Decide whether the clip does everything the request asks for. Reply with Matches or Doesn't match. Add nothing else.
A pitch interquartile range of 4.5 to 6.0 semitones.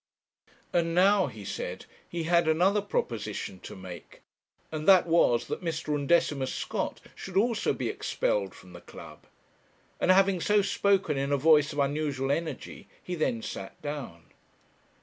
Matches